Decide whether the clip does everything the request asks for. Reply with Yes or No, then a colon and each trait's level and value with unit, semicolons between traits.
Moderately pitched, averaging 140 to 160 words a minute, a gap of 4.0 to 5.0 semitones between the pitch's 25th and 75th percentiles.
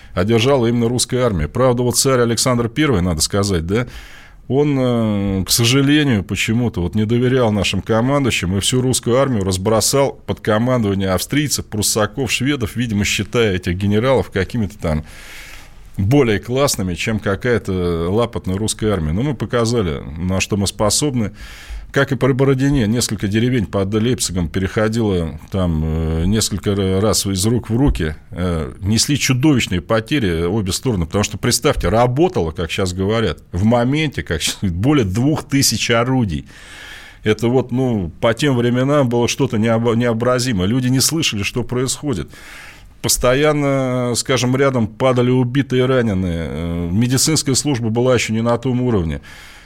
No: low, 115 Hz; average, 145 wpm; average, 4.7 semitones